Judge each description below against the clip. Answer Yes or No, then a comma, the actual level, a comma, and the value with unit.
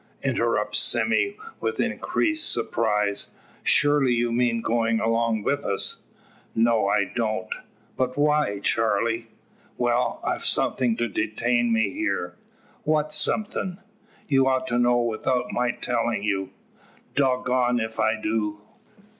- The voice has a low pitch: Yes, low, 120 Hz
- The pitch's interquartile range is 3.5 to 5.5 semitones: No, narrow, 2.5 semitones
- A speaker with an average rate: No, slow, 125 wpm